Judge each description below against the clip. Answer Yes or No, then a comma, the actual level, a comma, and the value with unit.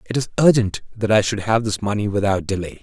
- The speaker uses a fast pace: Yes, fast, 235 wpm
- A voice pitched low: Yes, low, 105 Hz